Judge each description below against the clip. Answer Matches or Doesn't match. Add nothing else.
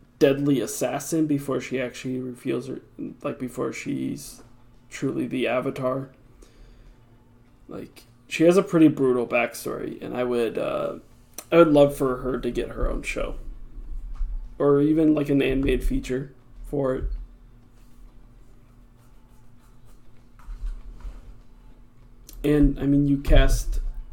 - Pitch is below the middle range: Matches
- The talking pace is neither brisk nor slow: Doesn't match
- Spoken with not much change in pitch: Matches